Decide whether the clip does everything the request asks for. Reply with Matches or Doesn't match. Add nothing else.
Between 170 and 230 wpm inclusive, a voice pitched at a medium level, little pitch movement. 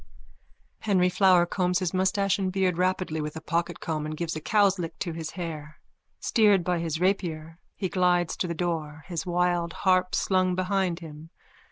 Matches